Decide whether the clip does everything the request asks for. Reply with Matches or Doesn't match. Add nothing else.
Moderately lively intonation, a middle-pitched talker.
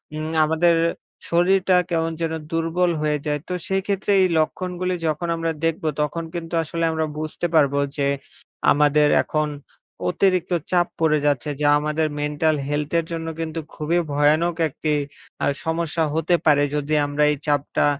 Doesn't match